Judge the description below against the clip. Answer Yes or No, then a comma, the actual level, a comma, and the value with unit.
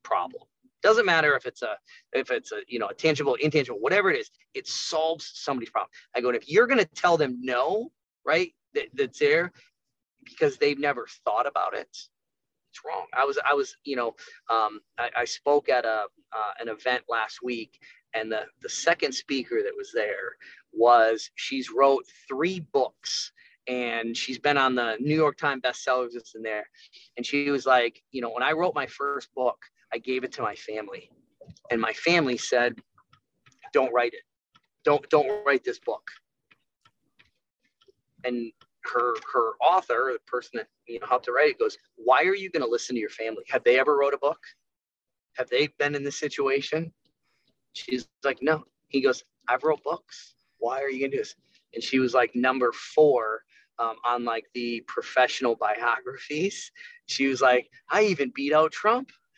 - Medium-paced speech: Yes, average, 185 wpm